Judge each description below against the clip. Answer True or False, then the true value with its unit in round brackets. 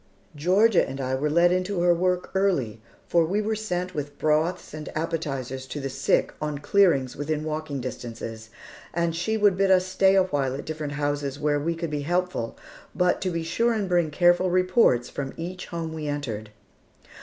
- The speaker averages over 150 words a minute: True (190 wpm)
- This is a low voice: False (160 Hz)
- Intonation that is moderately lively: True (4.1 semitones)